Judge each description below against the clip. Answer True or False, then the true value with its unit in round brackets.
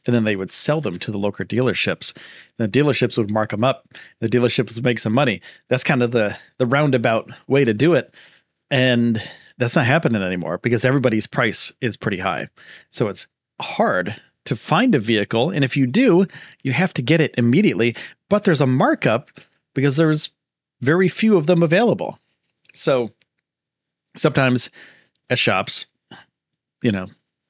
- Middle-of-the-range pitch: False (130 Hz)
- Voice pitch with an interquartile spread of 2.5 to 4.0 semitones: False (4.7 semitones)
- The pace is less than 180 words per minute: True (170 wpm)